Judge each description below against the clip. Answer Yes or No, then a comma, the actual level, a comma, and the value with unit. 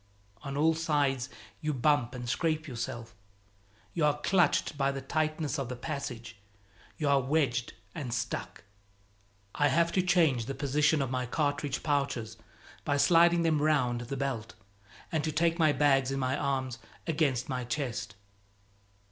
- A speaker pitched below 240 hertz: Yes, medium, 140 Hz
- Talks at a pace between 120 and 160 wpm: Yes, average, 155 wpm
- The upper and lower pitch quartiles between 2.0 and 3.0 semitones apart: No, average, 3.5 semitones